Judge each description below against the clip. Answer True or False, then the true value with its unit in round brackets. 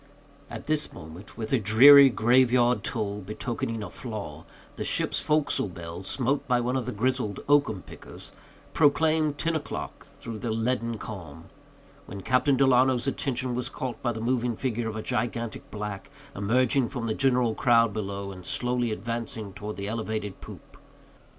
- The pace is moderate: True (165 wpm)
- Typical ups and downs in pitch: True (3.4 semitones)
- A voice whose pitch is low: True (115 Hz)